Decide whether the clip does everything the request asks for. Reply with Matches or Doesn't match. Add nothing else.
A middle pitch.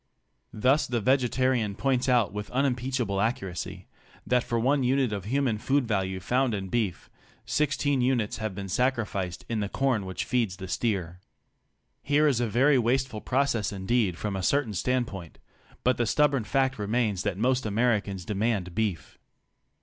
Doesn't match